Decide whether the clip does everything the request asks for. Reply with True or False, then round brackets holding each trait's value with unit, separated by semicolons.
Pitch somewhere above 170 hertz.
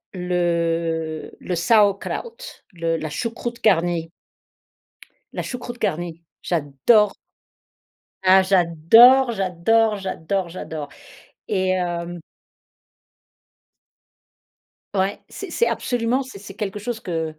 True (185 Hz)